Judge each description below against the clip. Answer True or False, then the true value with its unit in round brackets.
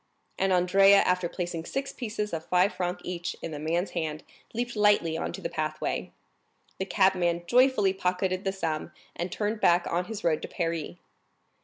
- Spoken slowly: False (175 wpm)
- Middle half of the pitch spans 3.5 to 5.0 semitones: False (2.9 semitones)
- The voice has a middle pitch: True (180 Hz)